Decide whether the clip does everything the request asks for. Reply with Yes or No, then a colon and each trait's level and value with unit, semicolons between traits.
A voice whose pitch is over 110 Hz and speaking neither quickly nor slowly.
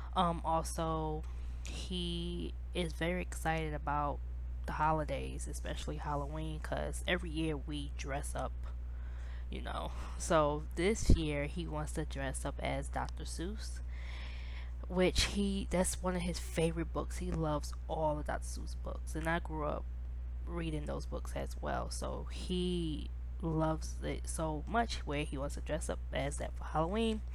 No: very low, 70 Hz; average, 155 wpm